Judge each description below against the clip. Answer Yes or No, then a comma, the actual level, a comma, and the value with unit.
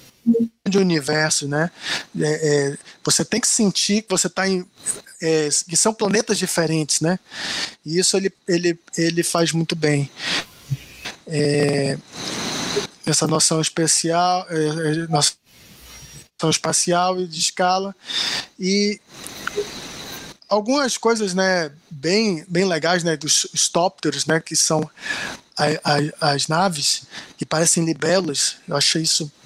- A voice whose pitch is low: No, medium, 165 Hz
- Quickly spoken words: No, average, 125 wpm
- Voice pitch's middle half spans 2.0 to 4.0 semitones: Yes, average, 3.6 semitones